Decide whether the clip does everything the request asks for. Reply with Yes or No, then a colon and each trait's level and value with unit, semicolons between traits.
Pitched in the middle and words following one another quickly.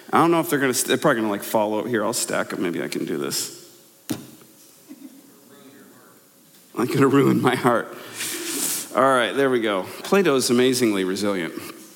No: medium, 165 Hz; average, 165 wpm